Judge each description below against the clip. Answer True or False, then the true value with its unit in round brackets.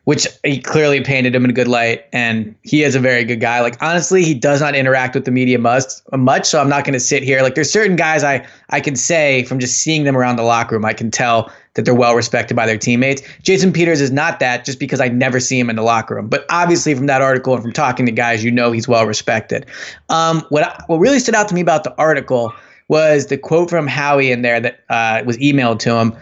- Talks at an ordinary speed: False (260 wpm)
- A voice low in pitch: True (130 Hz)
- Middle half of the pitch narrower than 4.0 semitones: True (3.6 semitones)